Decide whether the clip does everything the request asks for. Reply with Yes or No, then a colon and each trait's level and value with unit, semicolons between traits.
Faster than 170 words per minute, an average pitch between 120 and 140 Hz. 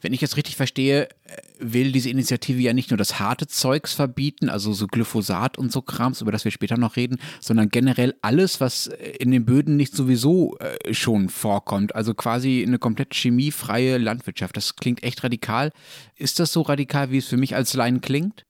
Yes: fast, 190 wpm; low, 125 Hz